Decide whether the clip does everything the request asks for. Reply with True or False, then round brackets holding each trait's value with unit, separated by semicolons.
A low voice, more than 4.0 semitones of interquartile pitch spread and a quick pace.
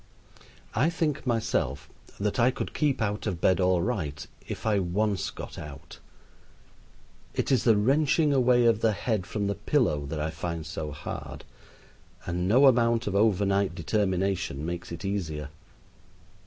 False (100 Hz; 5.5 semitones; 155 wpm)